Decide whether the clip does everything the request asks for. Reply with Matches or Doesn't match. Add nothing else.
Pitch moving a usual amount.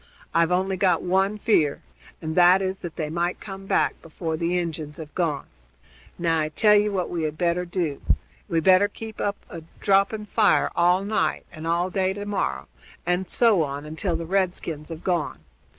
Matches